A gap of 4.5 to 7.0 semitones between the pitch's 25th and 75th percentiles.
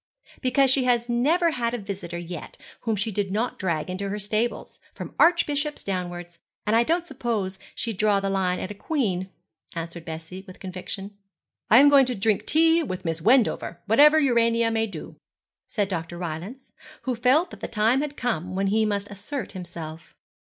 Yes: wide, 5.4 semitones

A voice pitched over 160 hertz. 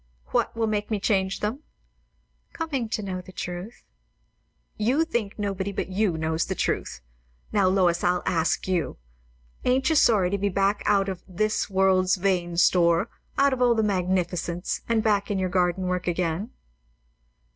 Yes: high, 190 Hz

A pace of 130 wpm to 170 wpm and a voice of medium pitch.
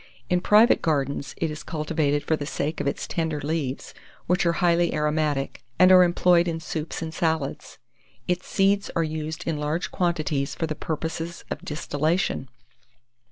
Yes: average, 160 wpm; medium, 160 Hz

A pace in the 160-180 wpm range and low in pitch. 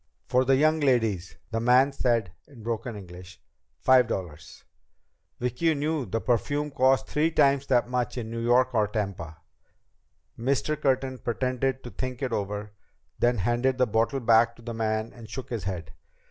Yes: average, 165 wpm; low, 120 Hz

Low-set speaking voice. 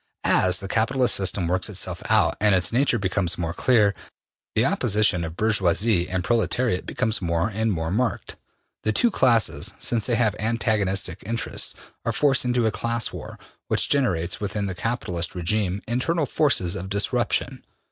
Yes: low, 105 Hz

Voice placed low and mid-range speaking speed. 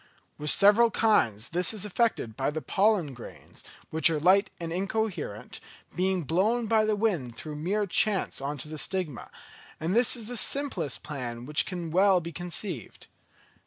No: medium, 180 Hz; average, 165 wpm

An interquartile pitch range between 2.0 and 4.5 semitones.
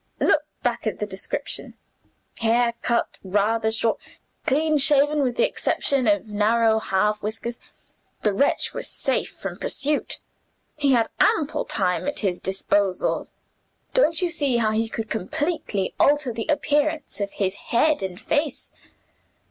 No: wide, 5.6 semitones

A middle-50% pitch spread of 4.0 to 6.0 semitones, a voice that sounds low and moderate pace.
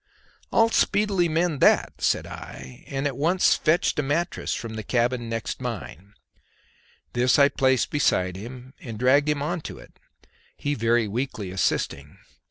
Yes: average, 4.6 semitones; low, 130 Hz; average, 155 wpm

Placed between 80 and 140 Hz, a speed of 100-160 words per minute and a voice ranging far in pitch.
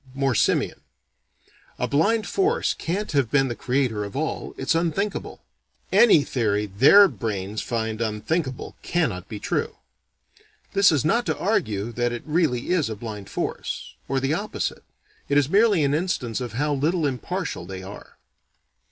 Yes: low, 135 Hz; average, 155 wpm; wide, 7.2 semitones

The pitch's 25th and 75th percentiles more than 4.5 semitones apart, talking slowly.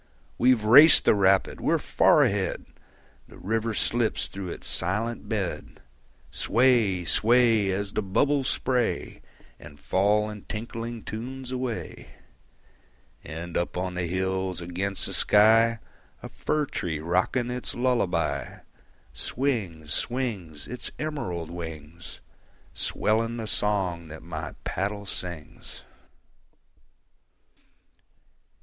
Yes: average, 4.9 semitones; slow, 110 wpm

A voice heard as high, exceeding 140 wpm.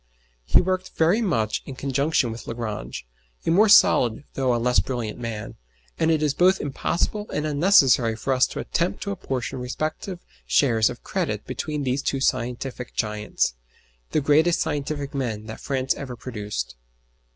No: low, 135 Hz; average, 160 wpm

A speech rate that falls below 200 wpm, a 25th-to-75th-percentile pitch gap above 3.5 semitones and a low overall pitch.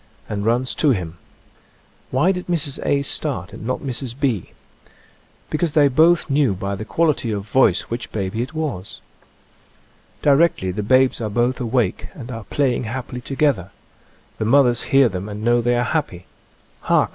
Yes: average, 170 wpm; average, 4.8 semitones; low, 125 Hz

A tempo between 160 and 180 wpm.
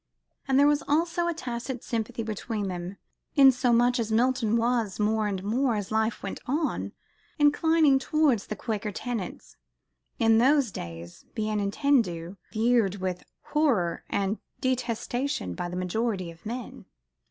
No: average, 140 wpm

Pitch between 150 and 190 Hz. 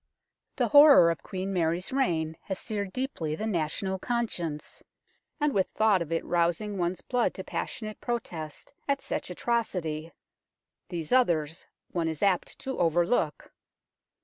Yes: medium, 185 Hz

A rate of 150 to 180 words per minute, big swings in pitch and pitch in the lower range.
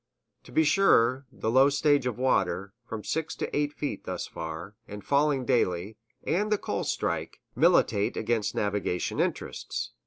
Yes: average, 155 wpm; wide, 6.2 semitones; low, 125 Hz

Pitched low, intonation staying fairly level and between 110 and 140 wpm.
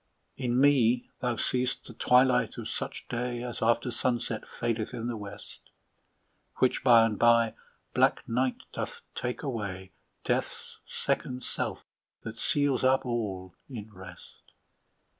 Yes: low, 120 Hz; narrow, 2.1 semitones; slow, 135 wpm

